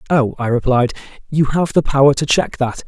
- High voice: No, low, 135 Hz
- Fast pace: Yes, fast, 210 wpm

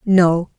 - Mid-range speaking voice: Yes, medium, 180 Hz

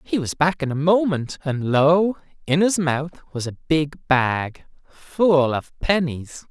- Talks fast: No, average, 165 wpm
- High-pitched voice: No, medium, 155 Hz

